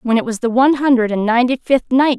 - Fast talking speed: Yes, fast, 275 wpm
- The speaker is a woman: Yes, female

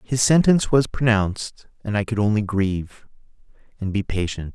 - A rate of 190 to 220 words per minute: No, average, 160 wpm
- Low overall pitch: Yes, low, 105 Hz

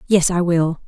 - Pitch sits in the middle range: Yes, medium, 175 Hz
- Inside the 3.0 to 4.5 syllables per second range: Yes, 4.3 syllables/s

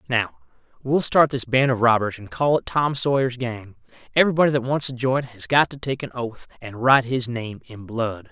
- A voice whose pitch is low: Yes, low, 125 Hz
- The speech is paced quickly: Yes, fast, 215 wpm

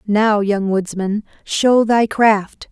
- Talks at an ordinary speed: No, slow, 130 wpm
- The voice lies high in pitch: Yes, high, 210 Hz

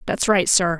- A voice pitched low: No, medium, 185 Hz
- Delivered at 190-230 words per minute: Yes, fast, 225 wpm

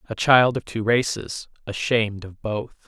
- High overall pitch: No, low, 110 Hz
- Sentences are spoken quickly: No, average, 165 wpm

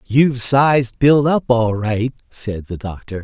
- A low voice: Yes, low, 120 Hz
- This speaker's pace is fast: No, average, 165 wpm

